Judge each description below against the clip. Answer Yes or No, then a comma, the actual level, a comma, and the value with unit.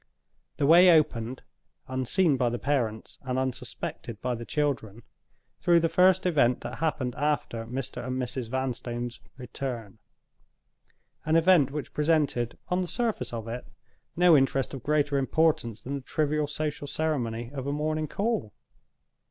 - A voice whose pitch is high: No, low, 135 Hz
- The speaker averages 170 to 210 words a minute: No, average, 145 wpm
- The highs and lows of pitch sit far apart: No, average, 4.2 semitones